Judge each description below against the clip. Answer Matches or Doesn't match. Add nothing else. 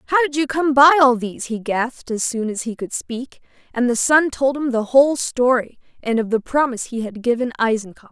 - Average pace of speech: Doesn't match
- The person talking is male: Doesn't match